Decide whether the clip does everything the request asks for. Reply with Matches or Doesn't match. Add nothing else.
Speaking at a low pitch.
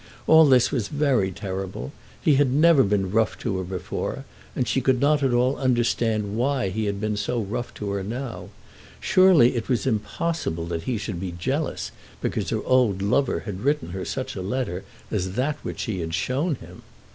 Matches